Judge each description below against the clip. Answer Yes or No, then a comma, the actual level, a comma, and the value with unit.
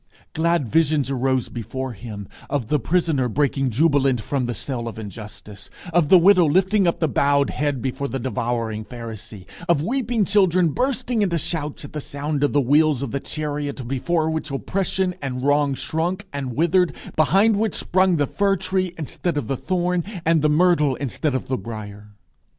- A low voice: No, medium, 145 Hz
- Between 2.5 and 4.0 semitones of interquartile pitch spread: No, average, 5.1 semitones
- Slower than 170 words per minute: No, average, 180 wpm